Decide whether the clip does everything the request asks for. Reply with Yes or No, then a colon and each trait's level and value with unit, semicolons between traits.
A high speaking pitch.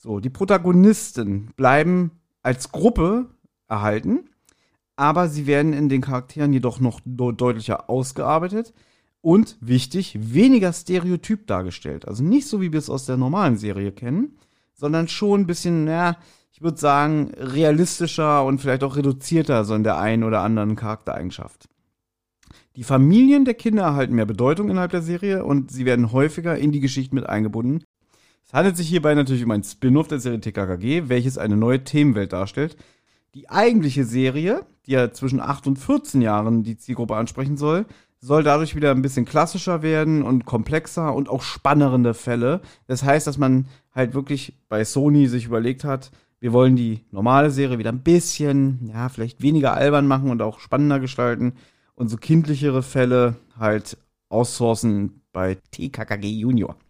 No: low, 135 Hz